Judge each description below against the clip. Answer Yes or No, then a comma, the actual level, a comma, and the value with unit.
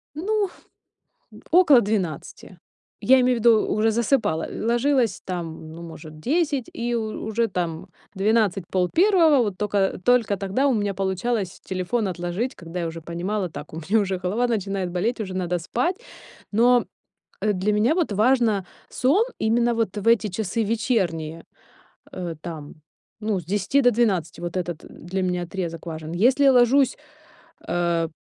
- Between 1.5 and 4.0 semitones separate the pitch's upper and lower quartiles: No, average, 5.2 semitones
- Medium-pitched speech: No, high, 205 Hz